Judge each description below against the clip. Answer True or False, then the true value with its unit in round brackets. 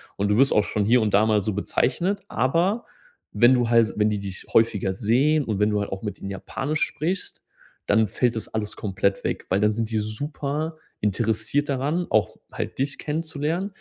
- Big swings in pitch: True (5.7 semitones)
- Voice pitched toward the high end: False (115 Hz)